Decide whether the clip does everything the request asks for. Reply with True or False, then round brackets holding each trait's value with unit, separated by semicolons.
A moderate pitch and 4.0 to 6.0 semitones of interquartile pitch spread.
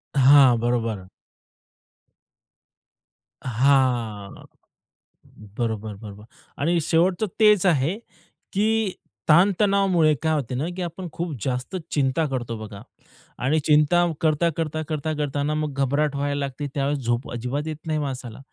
True (145 Hz; 4.6 semitones)